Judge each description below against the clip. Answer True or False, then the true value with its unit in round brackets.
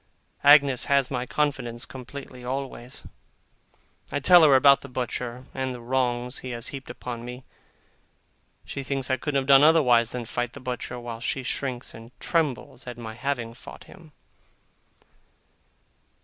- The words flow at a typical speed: True (155 wpm)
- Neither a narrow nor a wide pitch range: False (2.2 semitones)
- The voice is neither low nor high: False (130 Hz)